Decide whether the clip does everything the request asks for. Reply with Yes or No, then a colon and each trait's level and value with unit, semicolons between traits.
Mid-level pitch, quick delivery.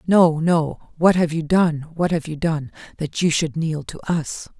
Yes: medium, 160 Hz; fast, 210 wpm